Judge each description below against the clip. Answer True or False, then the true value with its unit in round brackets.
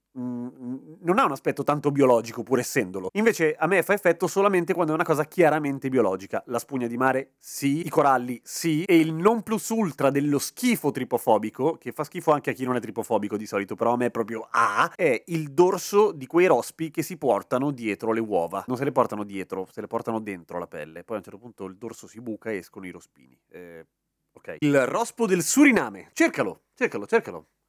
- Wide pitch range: True (6.3 semitones)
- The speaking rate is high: True (215 wpm)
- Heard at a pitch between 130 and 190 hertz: True (135 Hz)